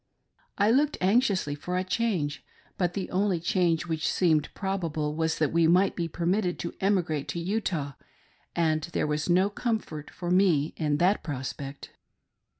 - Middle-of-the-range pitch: Yes, medium, 175 Hz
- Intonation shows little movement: No, average, 3.7 semitones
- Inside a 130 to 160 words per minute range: Yes, average, 155 wpm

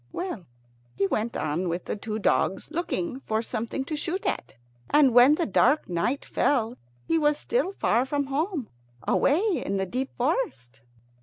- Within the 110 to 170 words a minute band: Yes, average, 165 wpm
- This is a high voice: Yes, very high, 265 Hz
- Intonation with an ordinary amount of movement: No, wide, 6.2 semitones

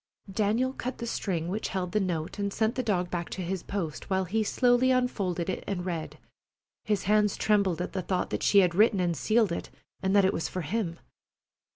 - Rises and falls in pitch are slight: No, average, 3.4 semitones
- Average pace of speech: No, fast, 215 wpm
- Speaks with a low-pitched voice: No, high, 195 Hz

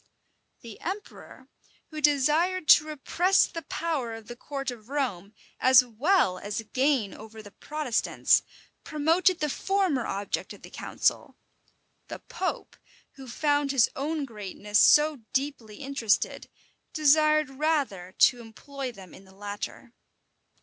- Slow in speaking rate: Yes, slow, 130 wpm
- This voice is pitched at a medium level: No, very high, 275 Hz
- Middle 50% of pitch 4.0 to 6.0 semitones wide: Yes, wide, 5.5 semitones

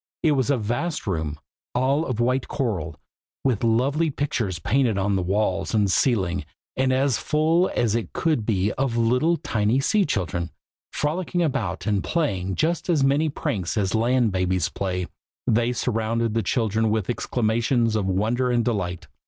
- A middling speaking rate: Yes, average, 160 wpm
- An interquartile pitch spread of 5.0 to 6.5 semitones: Yes, average, 5.3 semitones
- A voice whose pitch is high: No, low, 115 Hz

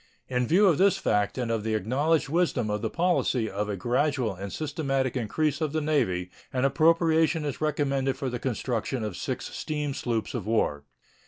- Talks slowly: No, average, 185 wpm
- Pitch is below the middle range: Yes, low, 130 Hz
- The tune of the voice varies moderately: No, wide, 5.7 semitones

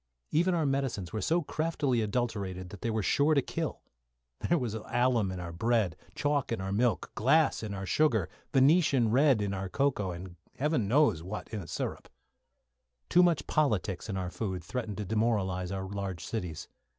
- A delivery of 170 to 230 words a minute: Yes, average, 180 wpm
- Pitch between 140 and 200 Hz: No, low, 110 Hz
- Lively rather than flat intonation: Yes, wide, 6.3 semitones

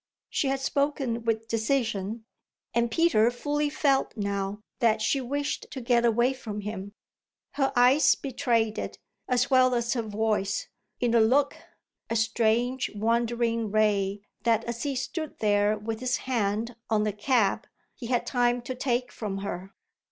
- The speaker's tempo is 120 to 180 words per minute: Yes, average, 155 wpm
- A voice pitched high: Yes, high, 235 Hz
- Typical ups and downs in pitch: Yes, average, 3.0 semitones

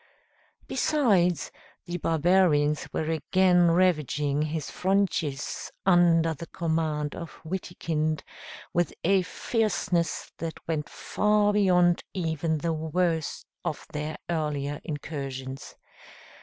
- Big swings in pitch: No, average, 3.0 semitones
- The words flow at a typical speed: No, slow, 100 wpm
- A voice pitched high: No, medium, 165 Hz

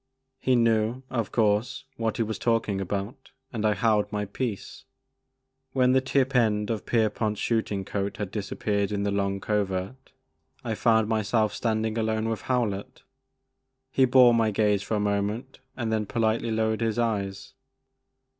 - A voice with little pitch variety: Yes, narrow, 2.2 semitones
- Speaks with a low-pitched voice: Yes, low, 110 Hz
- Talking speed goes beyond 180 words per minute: No, average, 160 wpm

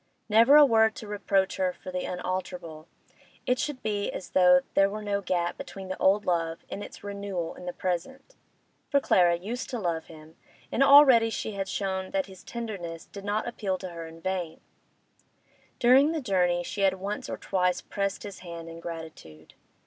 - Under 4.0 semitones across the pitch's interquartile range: Yes, average, 3.4 semitones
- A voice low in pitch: No, high, 190 Hz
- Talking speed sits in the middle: Yes, average, 185 wpm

